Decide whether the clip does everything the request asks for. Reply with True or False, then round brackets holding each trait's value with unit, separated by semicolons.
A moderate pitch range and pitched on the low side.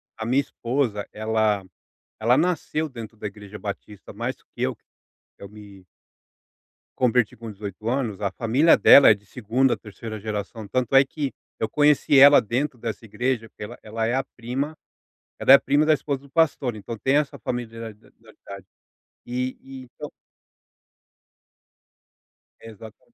True (4.0 semitones; 115 Hz)